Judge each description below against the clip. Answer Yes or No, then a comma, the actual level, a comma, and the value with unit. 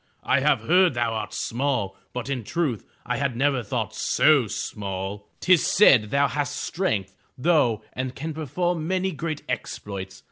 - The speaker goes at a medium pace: Yes, average, 155 wpm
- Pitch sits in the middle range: No, low, 130 Hz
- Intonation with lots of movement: Yes, wide, 6.2 semitones